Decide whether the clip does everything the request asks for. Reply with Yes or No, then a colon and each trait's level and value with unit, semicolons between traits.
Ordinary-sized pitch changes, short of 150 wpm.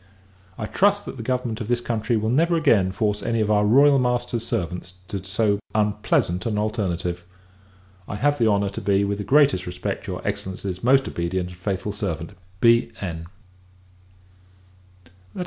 No: average, 4.3 semitones; average, 160 wpm